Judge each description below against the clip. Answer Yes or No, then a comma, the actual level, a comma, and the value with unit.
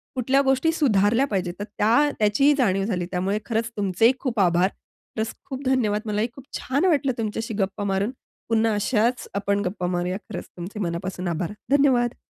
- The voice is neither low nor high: No, high, 215 Hz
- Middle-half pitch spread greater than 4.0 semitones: Yes, average, 4.8 semitones